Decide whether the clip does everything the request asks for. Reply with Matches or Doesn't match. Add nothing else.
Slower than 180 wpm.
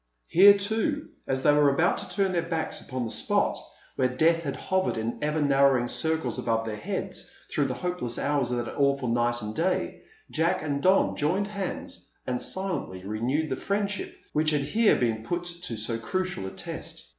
Doesn't match